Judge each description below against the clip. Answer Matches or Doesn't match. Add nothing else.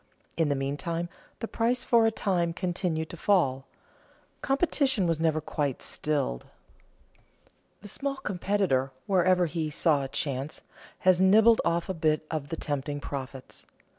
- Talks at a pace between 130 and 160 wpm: Matches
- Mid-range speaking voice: Matches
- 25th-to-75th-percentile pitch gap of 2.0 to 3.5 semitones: Doesn't match